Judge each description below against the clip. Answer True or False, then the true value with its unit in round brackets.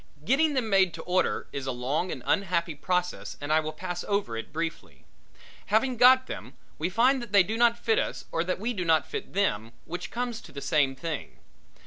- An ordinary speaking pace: False (210 wpm)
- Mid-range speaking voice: True (180 Hz)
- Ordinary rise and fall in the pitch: False (6.6 semitones)